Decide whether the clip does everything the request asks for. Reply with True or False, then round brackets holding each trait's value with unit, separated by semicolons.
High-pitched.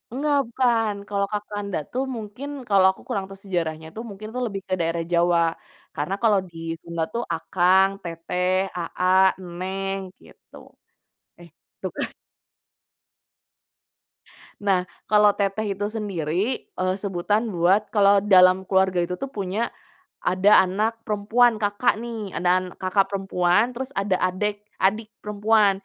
True (195 Hz)